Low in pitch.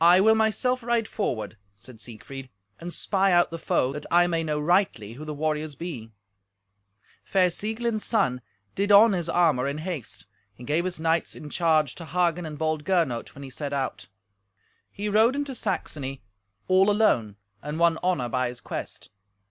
No: medium, 165 Hz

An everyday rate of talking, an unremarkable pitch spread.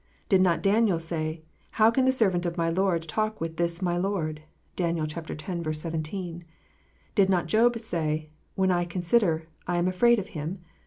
Yes: average, 175 wpm; average, 3.1 semitones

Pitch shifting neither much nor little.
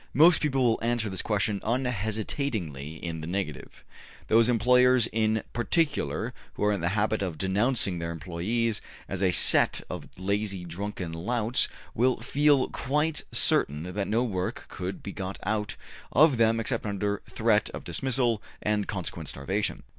Yes: average, 4.3 semitones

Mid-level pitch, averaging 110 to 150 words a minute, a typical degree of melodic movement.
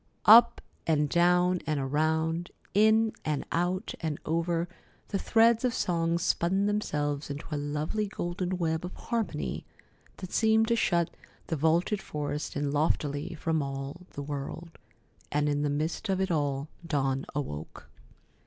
Yes: medium, 165 Hz; average, 145 wpm; average, 4.1 semitones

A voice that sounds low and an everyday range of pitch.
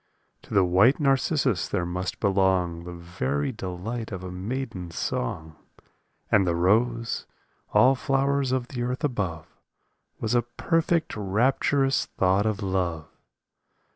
No: low, 100 Hz; wide, 6.0 semitones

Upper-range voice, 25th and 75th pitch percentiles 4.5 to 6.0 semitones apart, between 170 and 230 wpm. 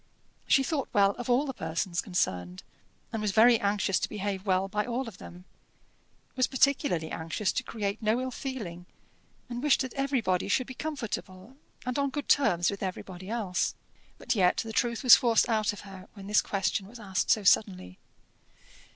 Yes: high, 210 Hz; average, 4.8 semitones; average, 180 wpm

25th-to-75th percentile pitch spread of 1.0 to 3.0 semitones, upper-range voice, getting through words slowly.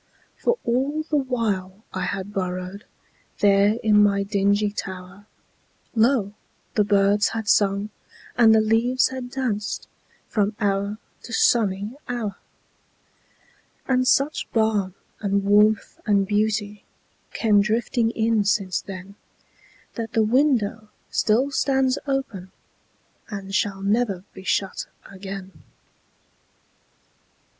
Yes: average, 2.7 semitones; high, 210 Hz; slow, 95 wpm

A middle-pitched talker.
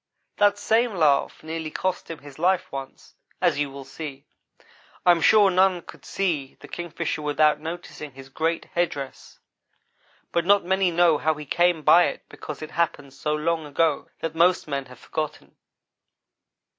Yes: medium, 160 Hz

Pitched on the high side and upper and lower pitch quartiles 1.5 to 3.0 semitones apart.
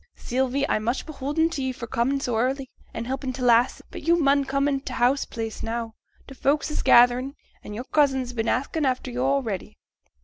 Yes: very high, 260 Hz; narrow, 2.5 semitones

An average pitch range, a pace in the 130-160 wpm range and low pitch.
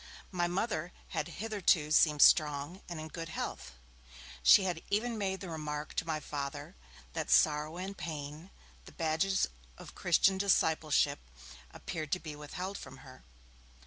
No: average, 3.8 semitones; average, 145 wpm; medium, 160 Hz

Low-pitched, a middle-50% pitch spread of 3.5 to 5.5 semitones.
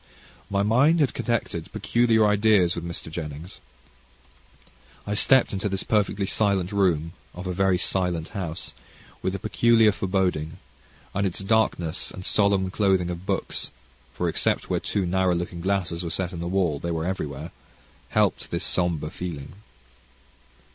No: very low, 95 Hz; average, 2.8 semitones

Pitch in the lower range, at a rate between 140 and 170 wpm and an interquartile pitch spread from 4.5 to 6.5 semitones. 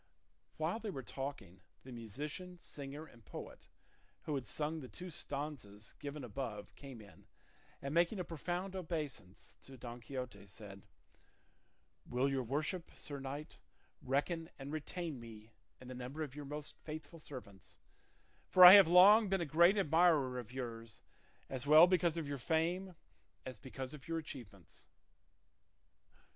No: medium, 145 Hz; average, 150 wpm; average, 4.8 semitones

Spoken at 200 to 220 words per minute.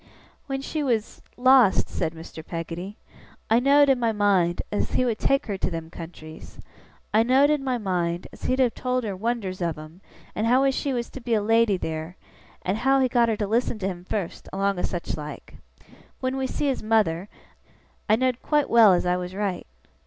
Yes: fast, 205 wpm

